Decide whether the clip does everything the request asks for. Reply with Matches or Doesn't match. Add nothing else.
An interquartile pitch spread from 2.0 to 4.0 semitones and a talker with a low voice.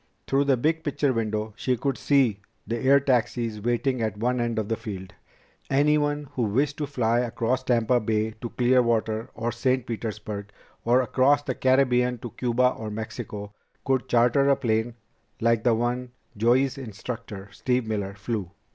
Matches